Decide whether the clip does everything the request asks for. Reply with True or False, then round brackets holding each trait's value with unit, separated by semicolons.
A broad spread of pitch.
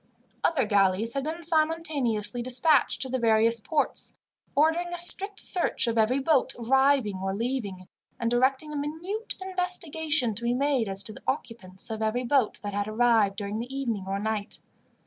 True (5.8 semitones)